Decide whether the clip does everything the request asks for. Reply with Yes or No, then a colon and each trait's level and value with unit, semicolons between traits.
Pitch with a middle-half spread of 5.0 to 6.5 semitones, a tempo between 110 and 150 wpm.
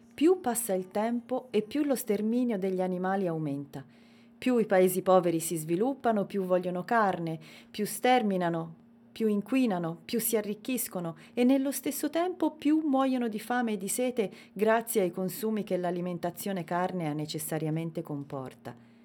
Yes: average, 5.3 semitones; average, 145 wpm